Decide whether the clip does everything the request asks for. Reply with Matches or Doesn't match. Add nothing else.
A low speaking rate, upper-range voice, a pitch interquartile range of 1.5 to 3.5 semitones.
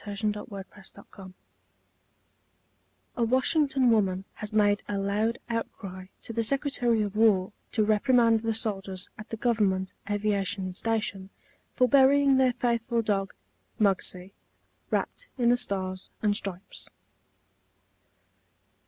Matches